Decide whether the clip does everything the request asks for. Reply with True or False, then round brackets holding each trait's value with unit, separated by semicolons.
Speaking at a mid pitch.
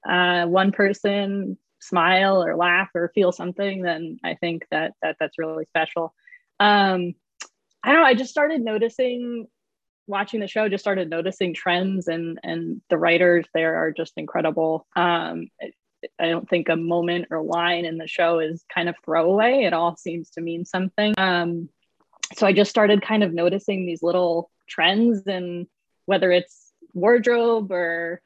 True (180 Hz)